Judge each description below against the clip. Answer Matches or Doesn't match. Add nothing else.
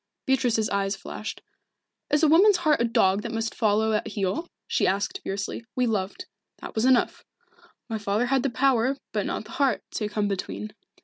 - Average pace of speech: Matches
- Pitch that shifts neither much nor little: Matches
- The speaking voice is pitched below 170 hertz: Doesn't match